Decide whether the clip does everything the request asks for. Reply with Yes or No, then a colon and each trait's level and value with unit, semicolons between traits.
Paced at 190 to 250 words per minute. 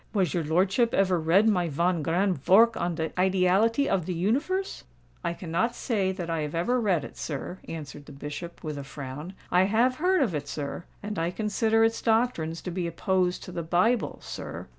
Yes: average, 195 wpm